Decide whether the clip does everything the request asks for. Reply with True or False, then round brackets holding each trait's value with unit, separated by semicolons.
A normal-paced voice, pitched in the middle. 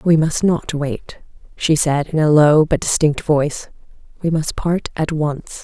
True (180 wpm; 155 Hz)